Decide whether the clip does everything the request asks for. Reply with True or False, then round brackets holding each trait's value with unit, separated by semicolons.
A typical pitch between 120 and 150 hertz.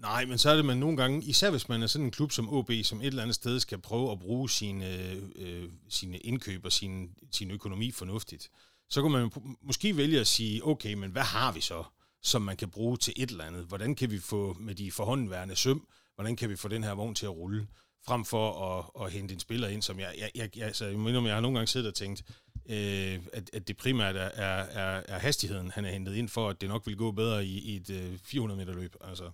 False (110 Hz)